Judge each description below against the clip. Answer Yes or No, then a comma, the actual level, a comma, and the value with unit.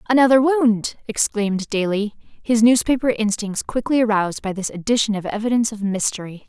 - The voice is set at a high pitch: Yes, high, 220 Hz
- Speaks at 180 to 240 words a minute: No, average, 150 wpm